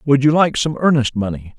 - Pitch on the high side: No, low, 135 Hz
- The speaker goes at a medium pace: No, fast, 225 wpm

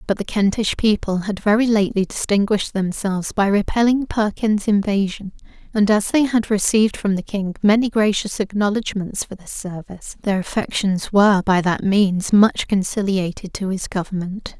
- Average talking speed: Yes, average, 155 wpm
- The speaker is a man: No, female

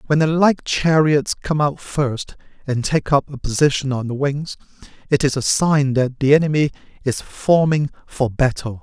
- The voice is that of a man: Yes, male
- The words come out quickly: No, average, 175 wpm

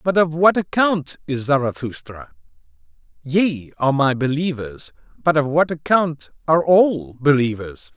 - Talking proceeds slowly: Yes, slow, 130 wpm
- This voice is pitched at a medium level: Yes, medium, 145 Hz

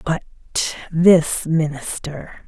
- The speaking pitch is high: No, medium, 160 Hz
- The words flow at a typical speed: No, slow, 75 wpm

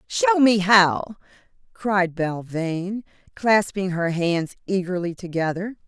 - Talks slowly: Yes, slow, 100 wpm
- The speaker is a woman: Yes, female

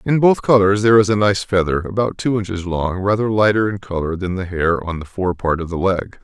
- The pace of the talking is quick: Yes, fast, 250 wpm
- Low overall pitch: Yes, very low, 95 Hz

